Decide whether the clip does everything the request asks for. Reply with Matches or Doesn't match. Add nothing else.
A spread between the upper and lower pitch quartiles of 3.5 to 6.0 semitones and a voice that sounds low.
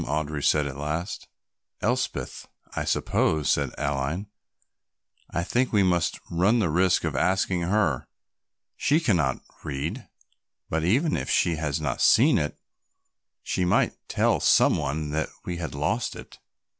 Matches